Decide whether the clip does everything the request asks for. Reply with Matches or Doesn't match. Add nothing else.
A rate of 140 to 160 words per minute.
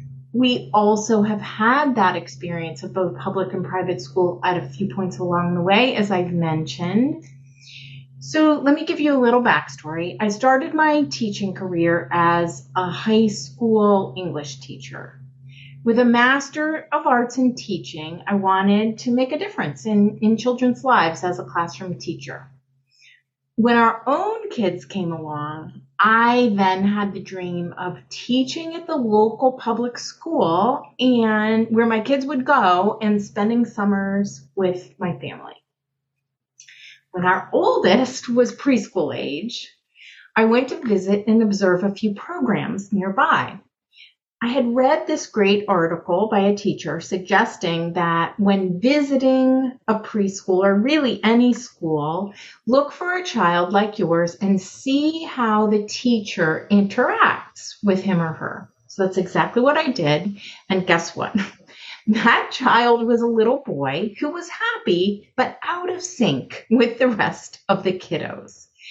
Matches